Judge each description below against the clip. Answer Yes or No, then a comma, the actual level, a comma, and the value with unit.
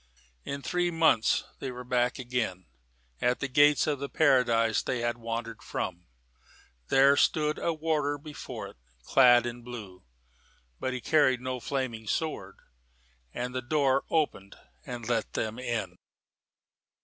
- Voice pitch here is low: Yes, low, 125 Hz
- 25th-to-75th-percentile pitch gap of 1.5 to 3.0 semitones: No, average, 3.4 semitones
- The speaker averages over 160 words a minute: No, average, 140 wpm